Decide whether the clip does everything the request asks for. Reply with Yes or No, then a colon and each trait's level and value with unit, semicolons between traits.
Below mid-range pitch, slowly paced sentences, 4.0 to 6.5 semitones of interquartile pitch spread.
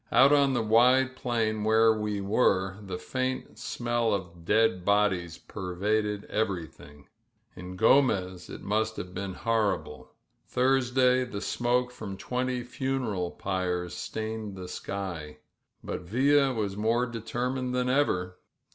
Yes: low, 110 Hz; slow, 120 wpm; average, 4.8 semitones